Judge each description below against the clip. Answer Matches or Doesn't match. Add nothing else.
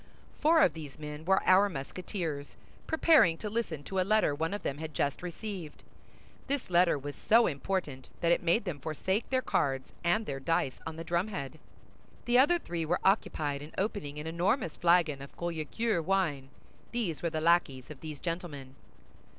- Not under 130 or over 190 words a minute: Matches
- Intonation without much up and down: Doesn't match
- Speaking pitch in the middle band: Matches